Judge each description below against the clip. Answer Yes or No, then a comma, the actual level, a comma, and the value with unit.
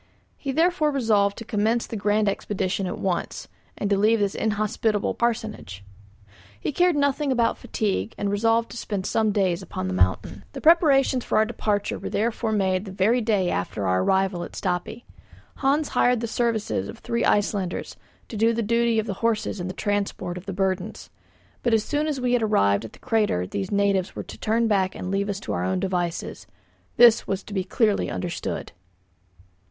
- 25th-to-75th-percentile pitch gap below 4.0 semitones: Yes, average, 3.5 semitones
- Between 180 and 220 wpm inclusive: Yes, average, 190 wpm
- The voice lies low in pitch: No, high, 210 Hz